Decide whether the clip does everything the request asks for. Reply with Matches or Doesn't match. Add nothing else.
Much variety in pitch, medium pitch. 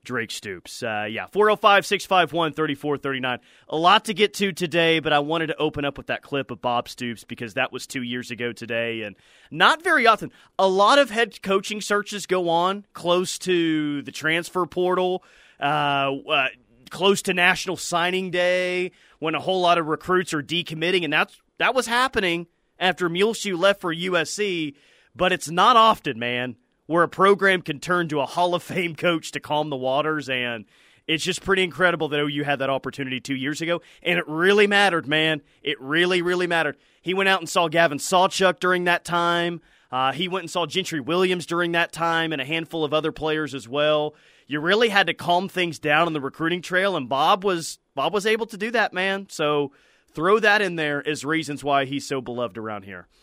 Doesn't match